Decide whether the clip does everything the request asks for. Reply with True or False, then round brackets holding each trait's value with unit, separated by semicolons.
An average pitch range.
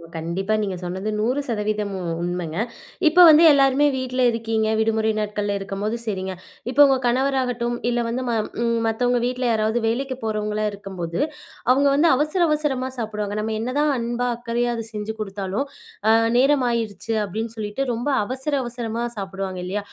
True (3.5 semitones)